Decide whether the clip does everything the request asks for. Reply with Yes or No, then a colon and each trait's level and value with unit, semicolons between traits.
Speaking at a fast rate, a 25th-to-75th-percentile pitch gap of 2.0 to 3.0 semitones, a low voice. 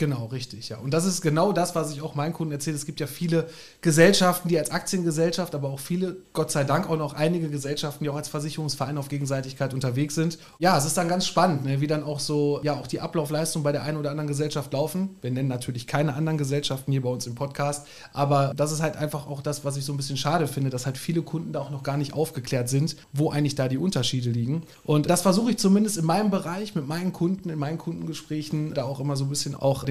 No: fast, 250 wpm; average, 2.7 semitones; medium, 150 Hz